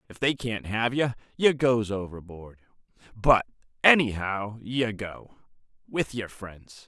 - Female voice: No, male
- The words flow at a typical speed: No, slow, 120 wpm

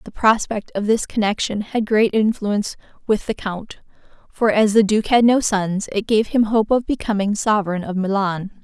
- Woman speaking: Yes, female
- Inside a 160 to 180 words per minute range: No, average, 190 wpm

